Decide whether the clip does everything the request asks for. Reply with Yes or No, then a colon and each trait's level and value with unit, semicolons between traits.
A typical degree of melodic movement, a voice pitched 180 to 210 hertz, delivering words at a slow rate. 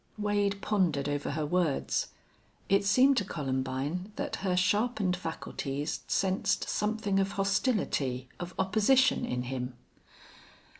No: wide, 6.1 semitones; medium, 185 Hz; slow, 115 wpm